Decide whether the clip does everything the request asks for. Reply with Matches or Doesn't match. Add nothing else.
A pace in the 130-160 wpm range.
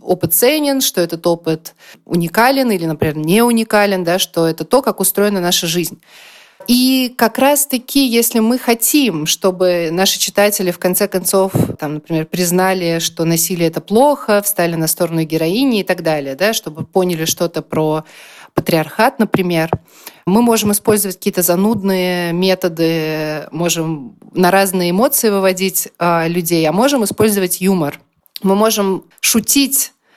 Matches